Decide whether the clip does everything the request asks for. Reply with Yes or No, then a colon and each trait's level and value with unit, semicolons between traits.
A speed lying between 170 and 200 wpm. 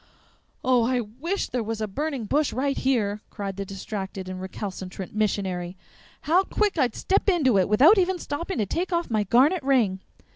Yes: average, 180 wpm